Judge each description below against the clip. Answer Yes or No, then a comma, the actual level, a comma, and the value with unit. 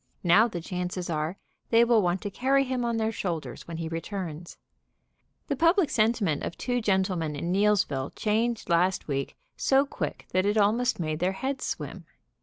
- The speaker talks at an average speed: Yes, average, 175 wpm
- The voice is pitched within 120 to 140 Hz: No, high, 195 Hz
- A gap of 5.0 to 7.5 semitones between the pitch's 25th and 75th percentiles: Yes, wide, 5.6 semitones